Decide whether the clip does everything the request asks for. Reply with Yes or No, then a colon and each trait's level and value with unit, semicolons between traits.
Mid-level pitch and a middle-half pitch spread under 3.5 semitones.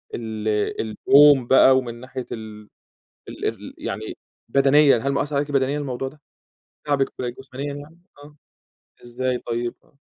No: low, 130 Hz; average, 3.0 semitones